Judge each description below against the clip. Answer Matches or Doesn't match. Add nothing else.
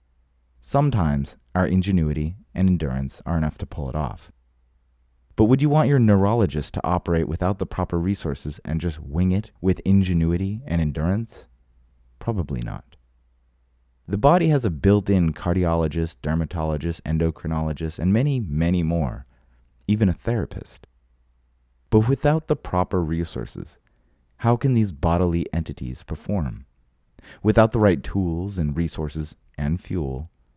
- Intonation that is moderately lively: Doesn't match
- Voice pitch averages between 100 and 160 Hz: Doesn't match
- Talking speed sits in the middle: Doesn't match